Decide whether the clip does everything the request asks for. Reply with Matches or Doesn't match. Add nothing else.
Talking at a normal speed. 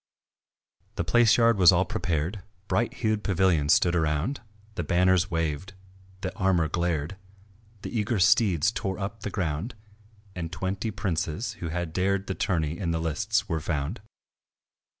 Matches